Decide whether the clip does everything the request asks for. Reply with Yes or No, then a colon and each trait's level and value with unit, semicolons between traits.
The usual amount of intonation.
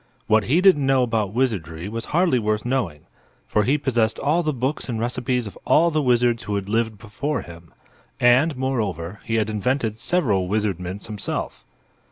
Yes: average, 4.1 semitones